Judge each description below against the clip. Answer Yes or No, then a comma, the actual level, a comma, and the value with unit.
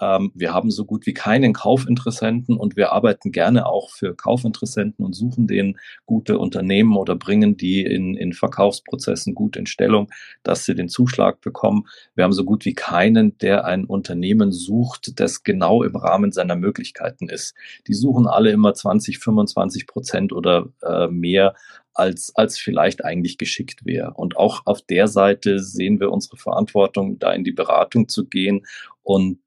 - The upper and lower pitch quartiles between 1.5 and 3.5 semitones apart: No, wide, 5.6 semitones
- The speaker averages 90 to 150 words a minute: No, average, 165 wpm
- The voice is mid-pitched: No, low, 110 Hz